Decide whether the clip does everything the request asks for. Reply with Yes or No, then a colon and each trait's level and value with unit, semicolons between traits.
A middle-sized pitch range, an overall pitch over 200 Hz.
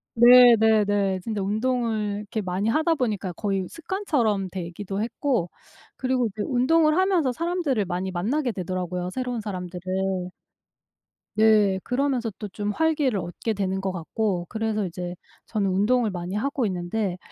Yes: average, 4.8 semitones; high, 210 Hz